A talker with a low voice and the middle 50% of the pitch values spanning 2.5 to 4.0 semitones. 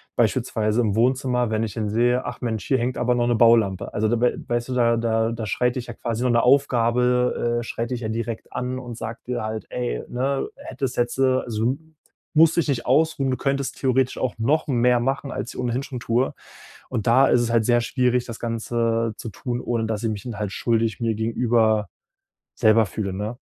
No: low, 120 Hz; narrow, 2.0 semitones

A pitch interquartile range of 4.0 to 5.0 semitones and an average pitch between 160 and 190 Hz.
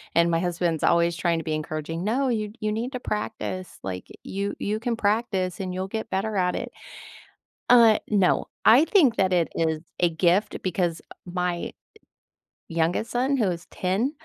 Yes: average, 4.4 semitones; medium, 185 Hz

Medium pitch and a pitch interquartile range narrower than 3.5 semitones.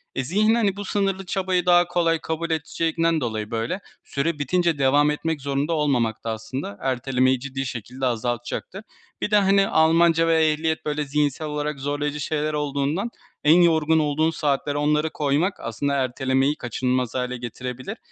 No: medium, 150 Hz; average, 3.8 semitones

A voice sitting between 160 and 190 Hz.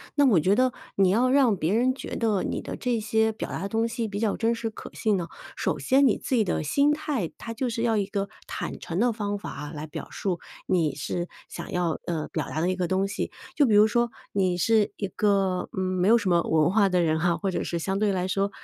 No: high, 200 Hz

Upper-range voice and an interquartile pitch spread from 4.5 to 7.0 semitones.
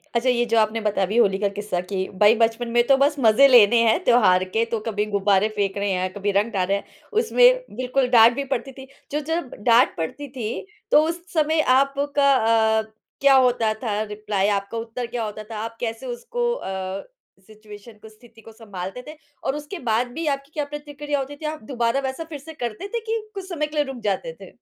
Yes: high, 235 Hz; average, 5.0 semitones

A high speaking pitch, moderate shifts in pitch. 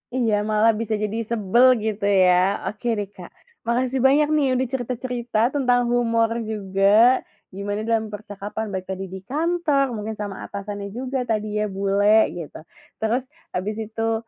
Yes: high, 220 Hz; average, 3.3 semitones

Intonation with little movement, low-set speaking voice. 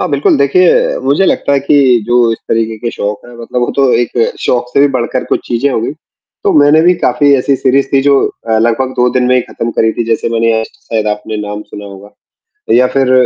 No: average, 3.4 semitones; low, 125 Hz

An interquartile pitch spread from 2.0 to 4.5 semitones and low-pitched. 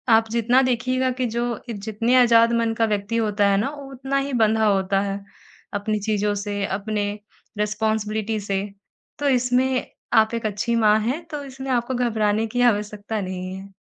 No: average, 3.1 semitones; high, 220 Hz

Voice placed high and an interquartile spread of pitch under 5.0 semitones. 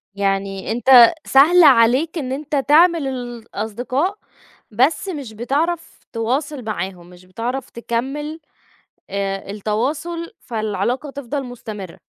No: very high, 250 Hz; wide, 5.5 semitones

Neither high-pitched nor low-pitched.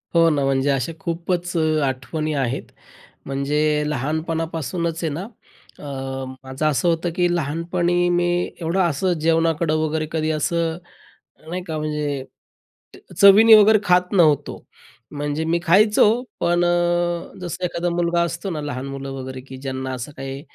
Yes: medium, 165 Hz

